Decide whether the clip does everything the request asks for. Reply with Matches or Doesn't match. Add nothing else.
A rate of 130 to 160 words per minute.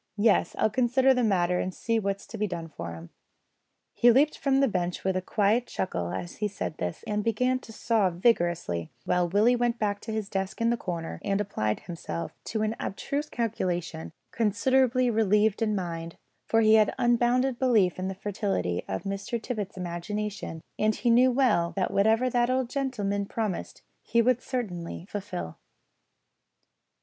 Doesn't match